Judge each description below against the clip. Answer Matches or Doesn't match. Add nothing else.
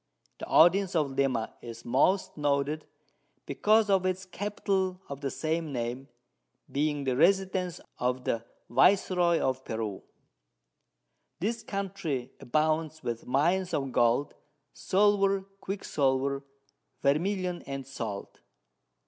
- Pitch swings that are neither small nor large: Doesn't match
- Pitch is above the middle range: Doesn't match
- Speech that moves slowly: Matches